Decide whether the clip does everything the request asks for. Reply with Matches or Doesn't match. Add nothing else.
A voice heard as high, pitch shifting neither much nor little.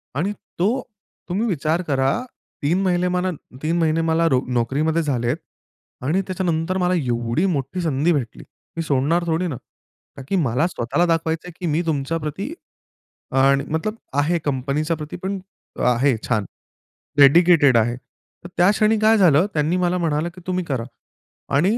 Doesn't match